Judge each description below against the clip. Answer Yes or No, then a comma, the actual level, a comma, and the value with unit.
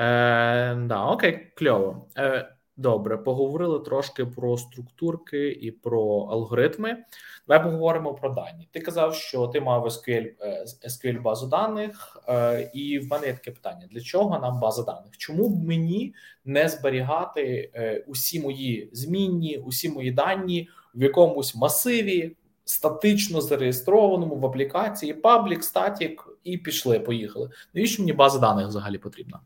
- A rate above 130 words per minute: Yes, average, 140 wpm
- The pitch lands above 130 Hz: Yes, medium, 140 Hz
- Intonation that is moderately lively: No, wide, 5.7 semitones